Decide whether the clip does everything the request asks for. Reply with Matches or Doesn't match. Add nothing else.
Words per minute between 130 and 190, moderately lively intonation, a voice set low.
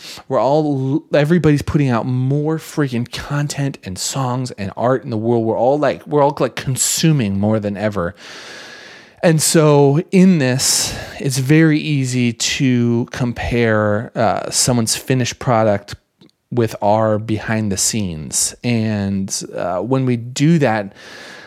Matches